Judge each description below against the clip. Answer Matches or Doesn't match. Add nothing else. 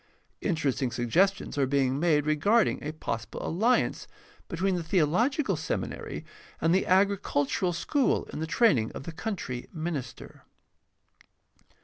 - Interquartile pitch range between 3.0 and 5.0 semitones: Doesn't match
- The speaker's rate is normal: Doesn't match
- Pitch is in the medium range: Matches